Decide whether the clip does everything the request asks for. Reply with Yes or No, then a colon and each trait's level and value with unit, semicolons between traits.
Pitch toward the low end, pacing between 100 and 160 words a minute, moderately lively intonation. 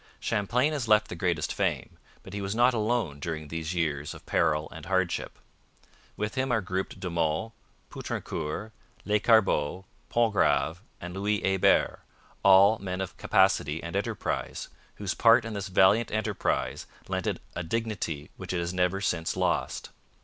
Yes: very low, 95 Hz; average, 155 wpm; average, 4.3 semitones